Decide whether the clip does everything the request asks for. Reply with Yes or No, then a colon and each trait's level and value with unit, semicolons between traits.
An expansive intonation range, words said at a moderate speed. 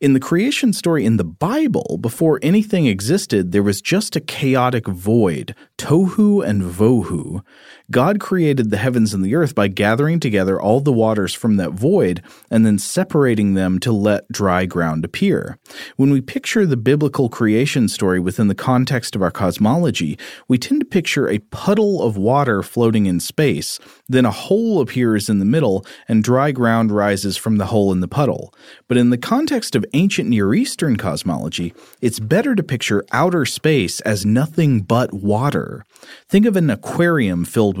Yes: wide, 7.7 semitones; average, 175 wpm